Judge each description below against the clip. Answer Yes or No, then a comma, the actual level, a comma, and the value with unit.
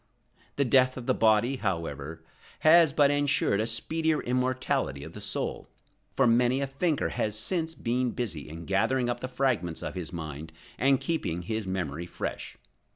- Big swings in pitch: Yes, wide, 7.4 semitones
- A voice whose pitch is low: Yes, low, 120 Hz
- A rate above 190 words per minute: No, average, 165 wpm